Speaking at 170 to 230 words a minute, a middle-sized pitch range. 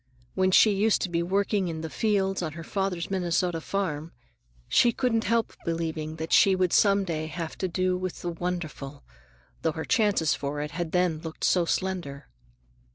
Yes: average, 180 wpm; average, 3.2 semitones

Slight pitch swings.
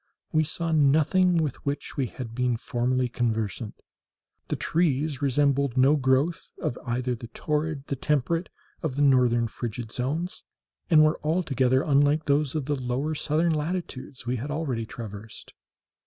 No: average, 3.7 semitones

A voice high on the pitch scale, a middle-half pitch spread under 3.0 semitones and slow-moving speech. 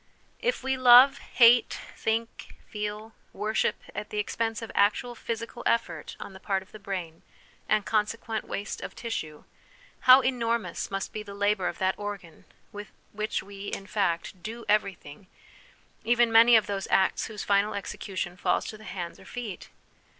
No: high, 210 Hz; narrow, 2.6 semitones; average, 165 wpm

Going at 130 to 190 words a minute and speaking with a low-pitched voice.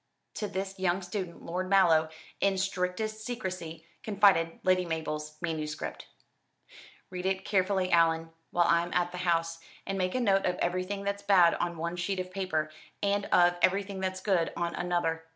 No: average, 165 wpm; medium, 180 Hz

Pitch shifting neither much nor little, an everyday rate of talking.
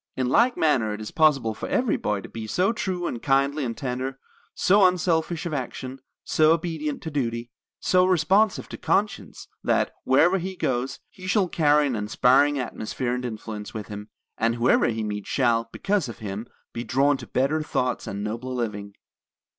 No: wide, 5.9 semitones; average, 180 wpm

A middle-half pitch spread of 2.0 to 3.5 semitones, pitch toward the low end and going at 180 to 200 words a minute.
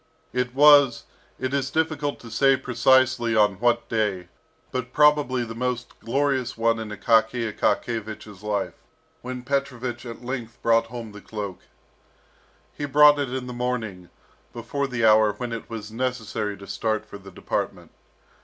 No: average, 3.0 semitones; low, 120 Hz; average, 155 wpm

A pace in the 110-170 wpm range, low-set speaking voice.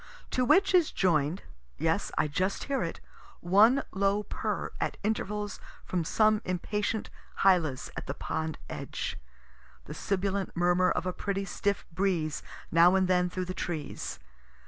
No: average, 145 wpm; high, 190 Hz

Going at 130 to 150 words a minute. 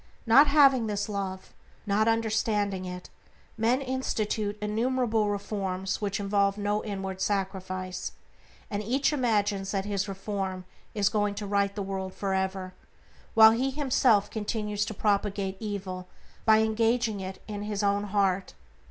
Yes: average, 140 wpm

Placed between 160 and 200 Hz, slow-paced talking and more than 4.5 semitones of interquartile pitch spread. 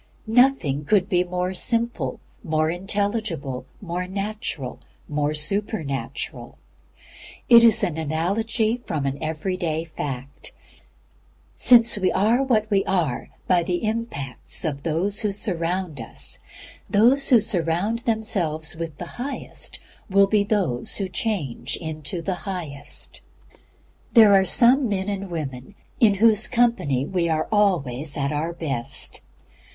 Yes: medium, 185 Hz; slow, 130 wpm; wide, 5.6 semitones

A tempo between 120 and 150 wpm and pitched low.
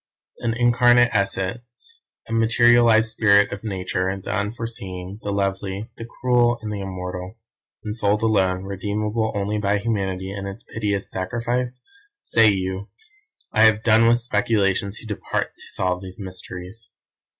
Yes: average, 140 wpm; low, 105 Hz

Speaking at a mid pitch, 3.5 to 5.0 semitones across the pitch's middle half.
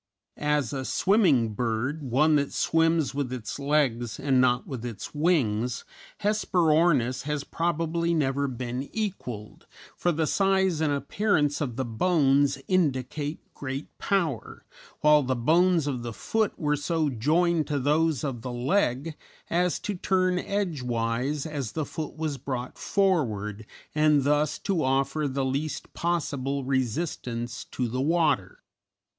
Yes: medium, 145 Hz; average, 4.3 semitones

